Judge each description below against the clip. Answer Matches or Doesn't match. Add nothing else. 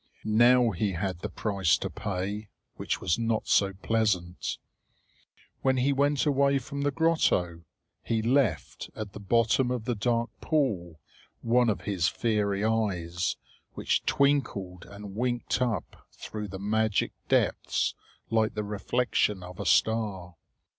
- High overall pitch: Doesn't match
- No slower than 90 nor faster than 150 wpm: Matches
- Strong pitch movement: Doesn't match